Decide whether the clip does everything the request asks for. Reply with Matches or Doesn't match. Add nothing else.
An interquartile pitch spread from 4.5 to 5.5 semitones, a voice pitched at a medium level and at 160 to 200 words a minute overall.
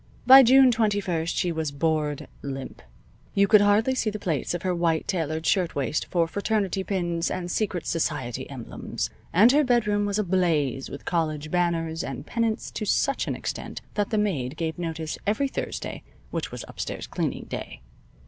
Matches